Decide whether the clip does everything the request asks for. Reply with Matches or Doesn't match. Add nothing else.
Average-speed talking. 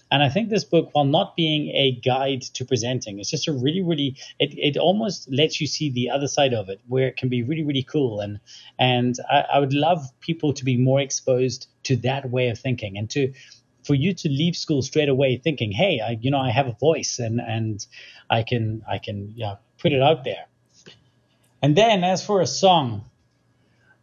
Doesn't match